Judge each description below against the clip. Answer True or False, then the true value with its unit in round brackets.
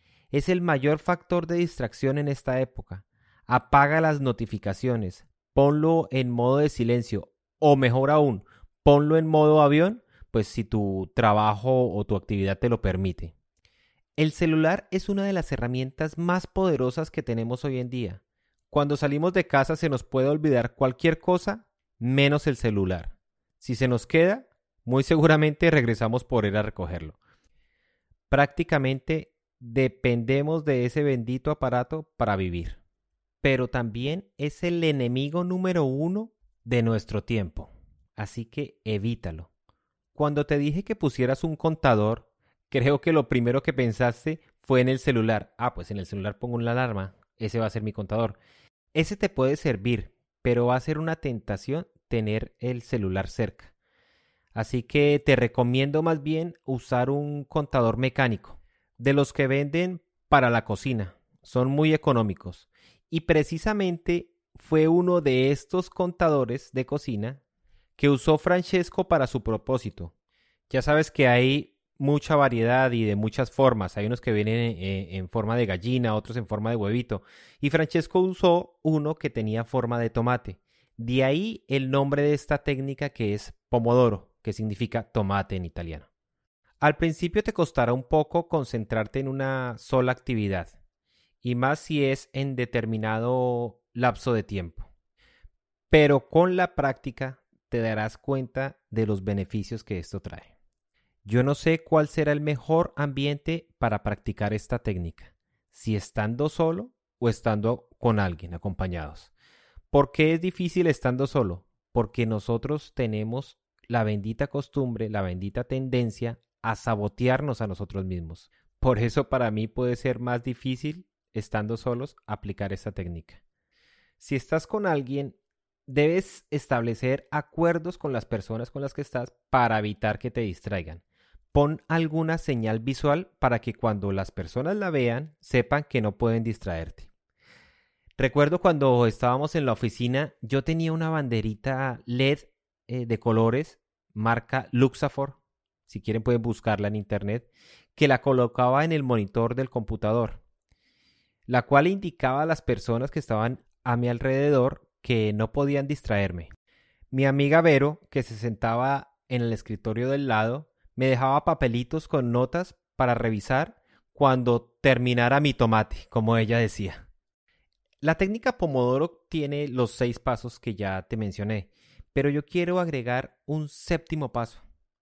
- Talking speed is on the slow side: False (145 wpm)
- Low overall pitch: True (125 Hz)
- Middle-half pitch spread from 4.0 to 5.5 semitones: True (4.9 semitones)